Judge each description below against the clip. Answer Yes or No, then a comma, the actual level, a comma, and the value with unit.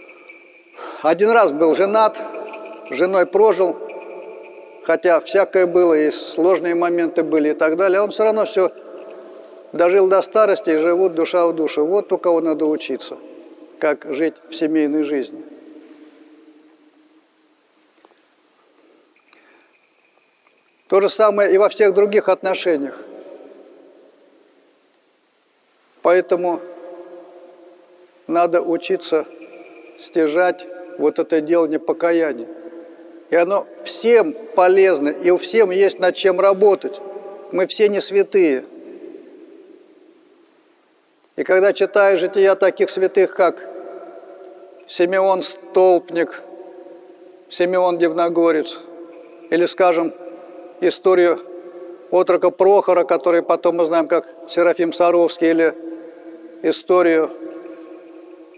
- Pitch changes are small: Yes, narrow, 2.3 semitones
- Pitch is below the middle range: No, medium, 175 Hz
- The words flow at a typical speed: No, slow, 100 wpm